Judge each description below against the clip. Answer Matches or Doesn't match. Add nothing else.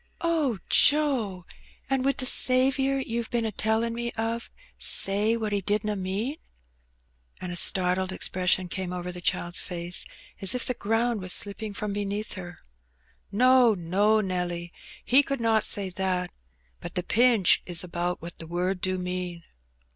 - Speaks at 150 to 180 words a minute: Matches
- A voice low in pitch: Doesn't match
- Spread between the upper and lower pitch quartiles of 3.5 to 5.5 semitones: Matches